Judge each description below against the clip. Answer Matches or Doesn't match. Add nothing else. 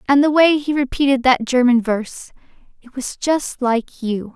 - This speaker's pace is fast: Doesn't match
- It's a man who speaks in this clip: Doesn't match